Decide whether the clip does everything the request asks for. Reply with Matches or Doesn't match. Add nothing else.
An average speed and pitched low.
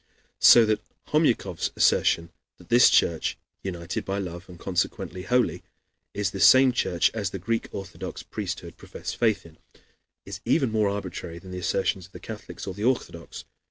Matches